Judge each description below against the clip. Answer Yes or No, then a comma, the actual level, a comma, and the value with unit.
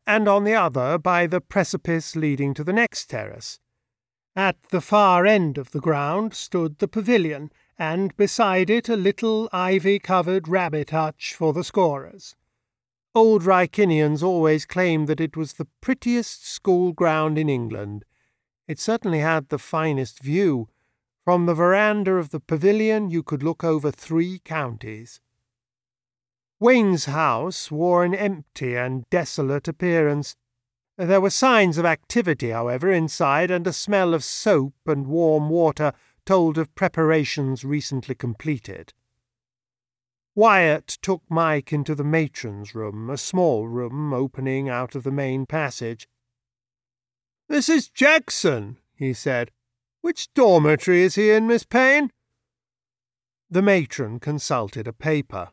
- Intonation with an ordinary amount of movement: No, wide, 6.5 semitones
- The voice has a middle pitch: Yes, medium, 155 Hz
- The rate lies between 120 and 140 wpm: Yes, slow, 135 wpm